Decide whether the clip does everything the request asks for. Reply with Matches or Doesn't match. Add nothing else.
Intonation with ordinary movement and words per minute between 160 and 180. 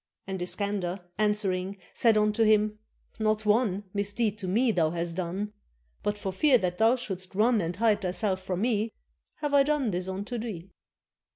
Matches